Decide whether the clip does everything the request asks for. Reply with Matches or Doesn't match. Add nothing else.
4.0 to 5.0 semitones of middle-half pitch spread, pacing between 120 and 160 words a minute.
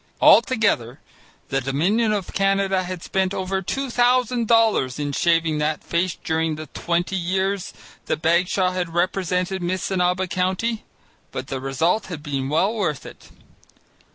Doesn't match